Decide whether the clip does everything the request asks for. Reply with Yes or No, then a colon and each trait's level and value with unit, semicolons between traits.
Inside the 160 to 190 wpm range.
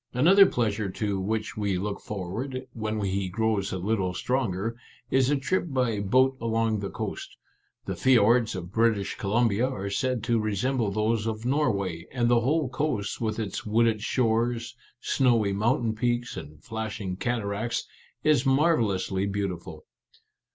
No: average, 150 wpm